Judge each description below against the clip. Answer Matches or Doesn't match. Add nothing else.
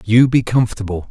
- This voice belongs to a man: Matches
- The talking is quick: Doesn't match